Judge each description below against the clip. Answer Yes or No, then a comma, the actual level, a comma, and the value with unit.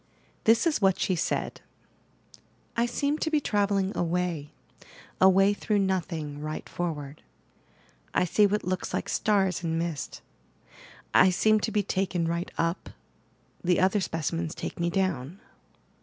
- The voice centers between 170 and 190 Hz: Yes, medium, 185 Hz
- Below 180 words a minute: Yes, average, 140 wpm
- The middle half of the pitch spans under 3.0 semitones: No, average, 3.4 semitones